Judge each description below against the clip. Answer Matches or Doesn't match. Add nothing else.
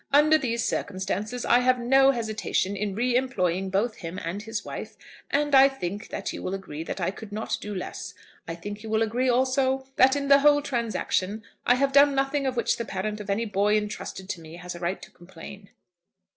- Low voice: Doesn't match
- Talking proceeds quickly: Matches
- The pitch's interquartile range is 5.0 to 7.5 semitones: Matches